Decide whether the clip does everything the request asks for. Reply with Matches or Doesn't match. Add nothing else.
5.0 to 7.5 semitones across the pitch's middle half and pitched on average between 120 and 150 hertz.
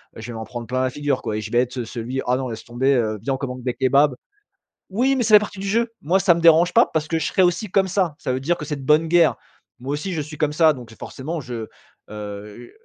Matches